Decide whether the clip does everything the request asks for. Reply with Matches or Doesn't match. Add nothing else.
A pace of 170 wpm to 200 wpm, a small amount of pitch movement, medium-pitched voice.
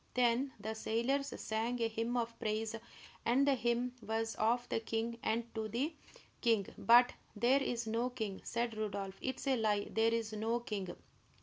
Doesn't match